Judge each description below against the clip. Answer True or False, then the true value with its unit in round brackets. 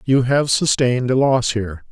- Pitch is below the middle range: True (125 Hz)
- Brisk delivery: False (190 wpm)